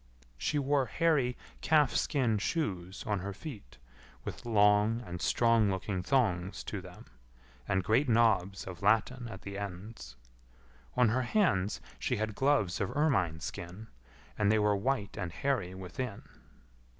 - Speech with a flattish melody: No, average, 4.8 semitones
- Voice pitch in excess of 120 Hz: No, low, 105 Hz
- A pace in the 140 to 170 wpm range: Yes, average, 145 wpm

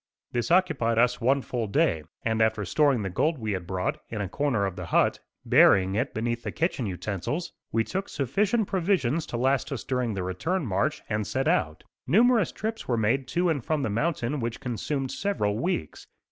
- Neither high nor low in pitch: No, low, 125 Hz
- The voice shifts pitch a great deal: Yes, wide, 6.6 semitones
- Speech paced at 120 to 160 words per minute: No, average, 195 wpm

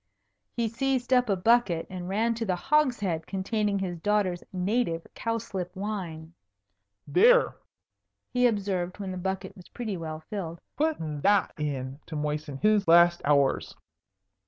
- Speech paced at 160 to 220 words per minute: No, average, 140 wpm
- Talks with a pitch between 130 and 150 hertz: No, high, 190 Hz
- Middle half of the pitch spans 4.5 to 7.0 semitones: Yes, average, 5.2 semitones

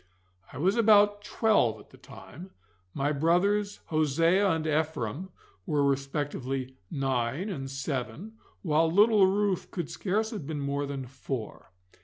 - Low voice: No, medium, 155 Hz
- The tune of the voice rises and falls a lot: Yes, wide, 6.4 semitones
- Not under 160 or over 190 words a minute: No, slow, 135 wpm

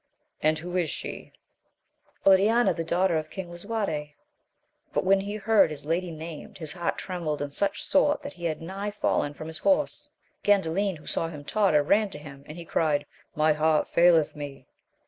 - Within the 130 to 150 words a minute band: No, average, 185 wpm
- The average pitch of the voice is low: No, medium, 170 Hz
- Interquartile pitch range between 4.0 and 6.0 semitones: Yes, average, 4.3 semitones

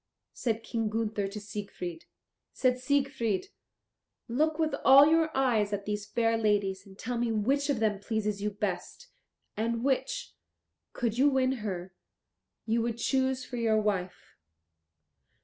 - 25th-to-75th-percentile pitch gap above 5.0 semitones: No, average, 4.1 semitones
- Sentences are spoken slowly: No, average, 145 wpm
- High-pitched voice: Yes, high, 225 Hz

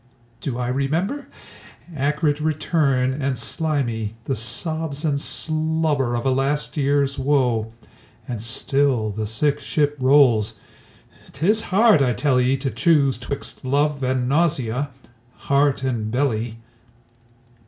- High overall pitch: No, medium, 140 Hz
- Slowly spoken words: Yes, slow, 120 wpm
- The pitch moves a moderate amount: Yes, average, 3.2 semitones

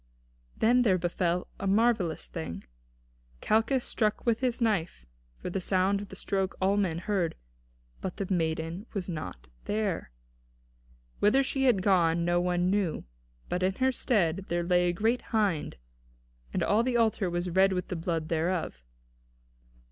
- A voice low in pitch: No, high, 190 Hz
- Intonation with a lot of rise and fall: No, average, 3.6 semitones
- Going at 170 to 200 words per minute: No, average, 155 wpm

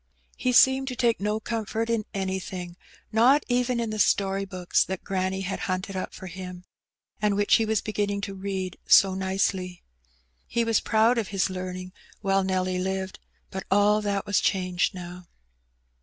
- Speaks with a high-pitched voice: Yes, high, 195 Hz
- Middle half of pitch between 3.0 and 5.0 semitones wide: No, narrow, 2.6 semitones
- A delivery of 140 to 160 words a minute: No, average, 170 wpm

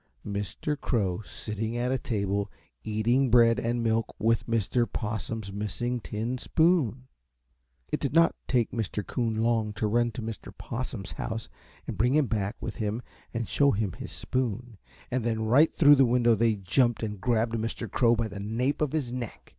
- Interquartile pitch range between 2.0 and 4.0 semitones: Yes, narrow, 2.6 semitones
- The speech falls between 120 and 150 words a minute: No, average, 180 wpm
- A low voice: Yes, low, 115 Hz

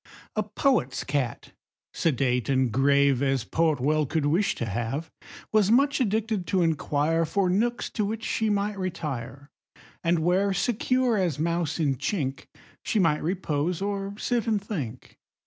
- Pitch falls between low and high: Yes, medium, 165 Hz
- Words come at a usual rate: Yes, average, 150 wpm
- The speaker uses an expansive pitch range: Yes, wide, 6.4 semitones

